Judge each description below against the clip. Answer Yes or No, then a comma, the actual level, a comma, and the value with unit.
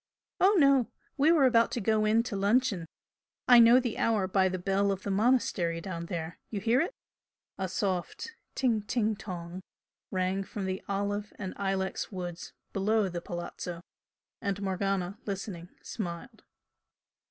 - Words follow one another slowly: No, average, 155 wpm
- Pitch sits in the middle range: No, high, 200 Hz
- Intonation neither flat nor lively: Yes, average, 3.4 semitones